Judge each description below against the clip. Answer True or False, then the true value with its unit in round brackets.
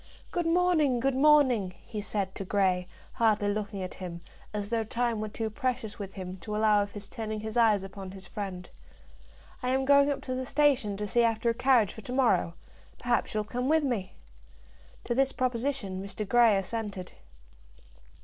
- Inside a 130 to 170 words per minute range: False (185 wpm)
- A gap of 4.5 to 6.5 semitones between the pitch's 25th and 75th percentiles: False (4.1 semitones)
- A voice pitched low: False (220 Hz)